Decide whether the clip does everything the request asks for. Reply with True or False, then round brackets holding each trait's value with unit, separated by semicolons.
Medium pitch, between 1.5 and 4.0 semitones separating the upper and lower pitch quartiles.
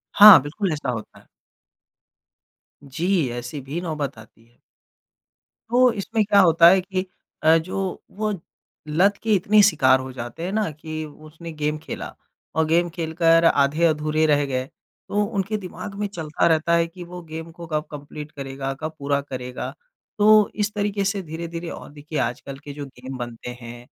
False (160 Hz; 4.7 semitones)